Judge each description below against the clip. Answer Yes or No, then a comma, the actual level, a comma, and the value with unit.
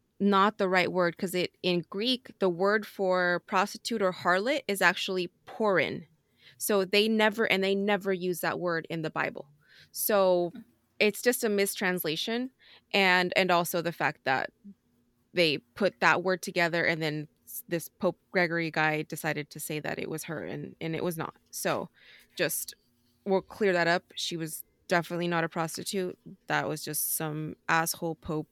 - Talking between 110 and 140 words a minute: No, average, 170 wpm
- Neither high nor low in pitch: Yes, medium, 180 Hz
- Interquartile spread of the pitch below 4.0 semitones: Yes, average, 3.3 semitones